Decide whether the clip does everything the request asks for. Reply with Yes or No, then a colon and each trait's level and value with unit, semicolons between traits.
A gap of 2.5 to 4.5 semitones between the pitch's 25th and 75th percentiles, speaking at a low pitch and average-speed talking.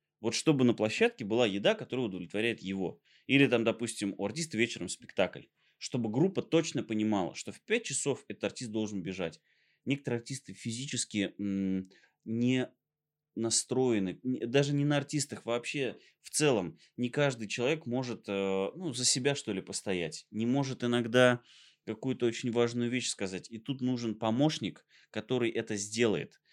Yes: average, 3.6 semitones; low, 120 Hz; average, 150 wpm